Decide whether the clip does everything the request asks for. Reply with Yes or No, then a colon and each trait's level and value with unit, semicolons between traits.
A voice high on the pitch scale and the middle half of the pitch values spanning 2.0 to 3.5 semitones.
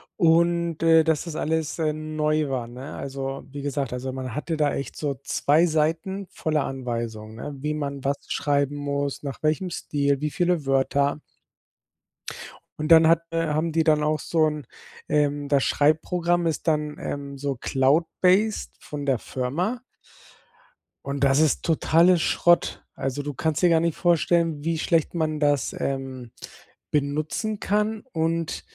No: medium, 150 Hz; average, 2.8 semitones